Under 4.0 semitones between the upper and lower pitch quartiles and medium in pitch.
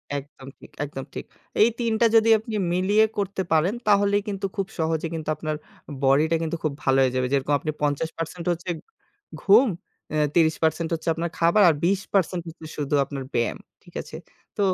No: average, 4.6 semitones; medium, 165 Hz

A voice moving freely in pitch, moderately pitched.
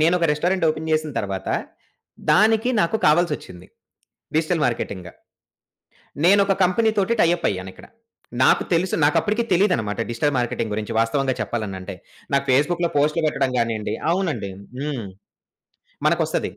Yes: wide, 7.5 semitones; medium, 150 Hz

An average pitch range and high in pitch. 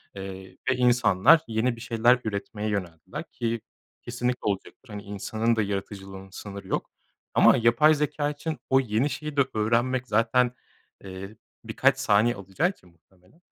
No: average, 4.2 semitones; low, 115 Hz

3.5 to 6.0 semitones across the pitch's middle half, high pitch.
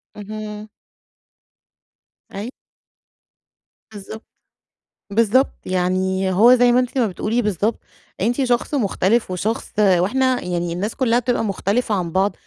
Yes: average, 4.2 semitones; high, 210 Hz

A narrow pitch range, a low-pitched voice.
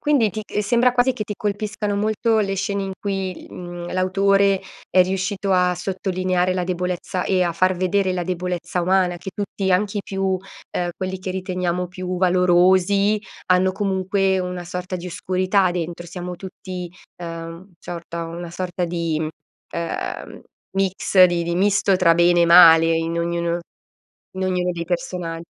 No: narrow, 1.8 semitones; medium, 185 Hz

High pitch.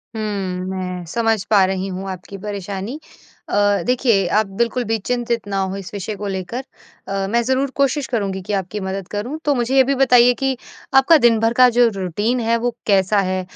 Yes: high, 215 Hz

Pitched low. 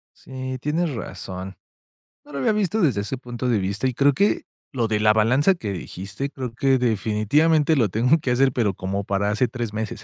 Yes: low, 125 Hz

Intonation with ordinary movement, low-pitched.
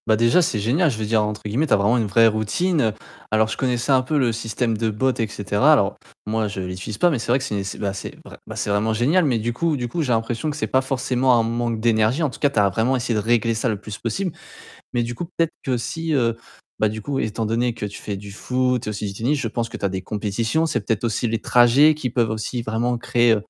Yes: average, 3.1 semitones; low, 115 Hz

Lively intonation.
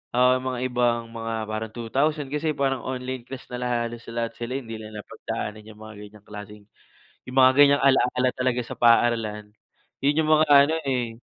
No: average, 2.7 semitones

